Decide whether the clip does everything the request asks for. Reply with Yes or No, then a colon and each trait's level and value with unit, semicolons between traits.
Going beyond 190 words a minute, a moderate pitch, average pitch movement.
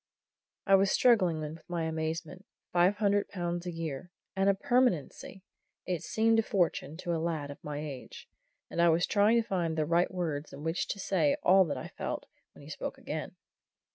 Yes: average, 200 wpm; medium, 175 Hz; average, 3.5 semitones